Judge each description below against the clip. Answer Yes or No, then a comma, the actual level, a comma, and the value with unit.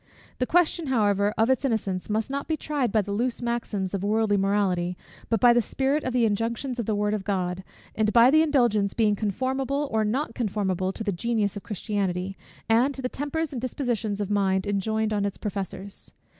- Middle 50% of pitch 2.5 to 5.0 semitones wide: Yes, average, 3.9 semitones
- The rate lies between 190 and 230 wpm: Yes, average, 200 wpm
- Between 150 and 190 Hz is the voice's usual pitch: No, high, 220 Hz